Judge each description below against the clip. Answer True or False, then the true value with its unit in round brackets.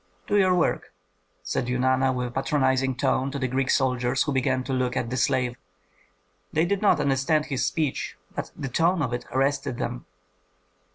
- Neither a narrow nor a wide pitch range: False (2.2 semitones)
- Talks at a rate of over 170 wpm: True (180 wpm)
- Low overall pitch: True (130 Hz)